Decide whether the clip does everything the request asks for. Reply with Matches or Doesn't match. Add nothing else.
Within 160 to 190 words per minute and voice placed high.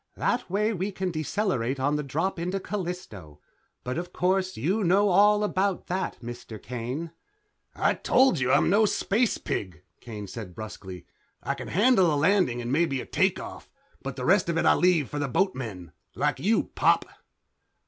Doesn't match